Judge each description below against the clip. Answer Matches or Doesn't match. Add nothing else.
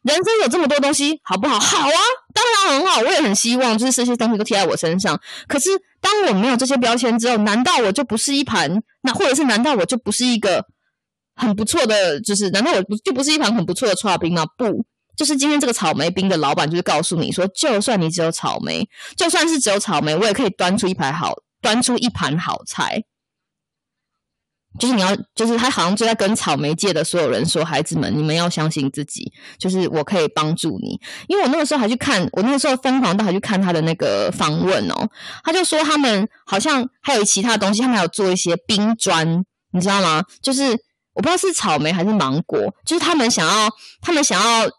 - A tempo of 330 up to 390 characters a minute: Matches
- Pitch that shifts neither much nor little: Doesn't match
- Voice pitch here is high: Matches